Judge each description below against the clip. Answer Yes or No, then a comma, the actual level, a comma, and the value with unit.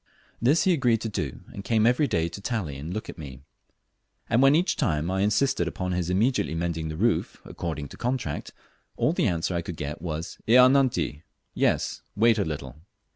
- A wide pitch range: Yes, wide, 6.8 semitones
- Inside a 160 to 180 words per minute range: No, average, 195 wpm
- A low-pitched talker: Yes, very low, 95 Hz